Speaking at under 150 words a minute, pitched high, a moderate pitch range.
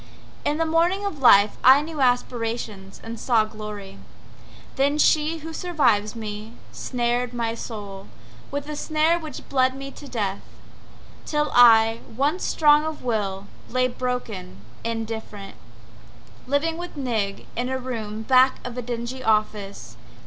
Yes: average, 140 wpm; high, 245 Hz; average, 4.9 semitones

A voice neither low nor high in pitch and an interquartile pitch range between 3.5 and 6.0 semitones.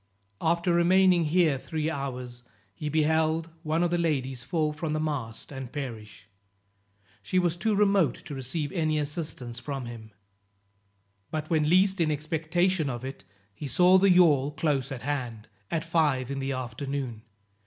Yes: medium, 150 Hz; average, 4.0 semitones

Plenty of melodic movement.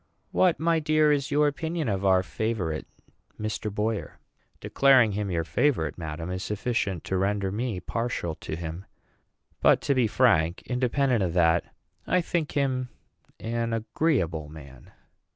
Yes: wide, 7.3 semitones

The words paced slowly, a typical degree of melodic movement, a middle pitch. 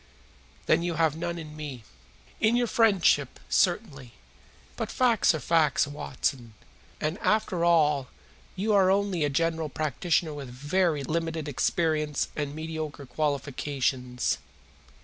Yes: slow, 125 wpm; average, 3.3 semitones; medium, 155 Hz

